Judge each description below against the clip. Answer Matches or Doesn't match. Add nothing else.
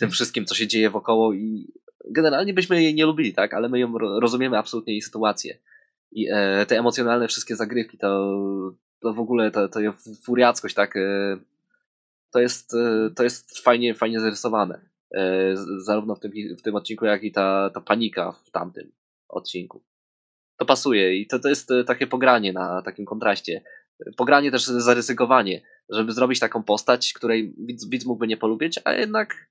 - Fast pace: Matches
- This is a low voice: Matches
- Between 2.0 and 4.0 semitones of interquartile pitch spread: Matches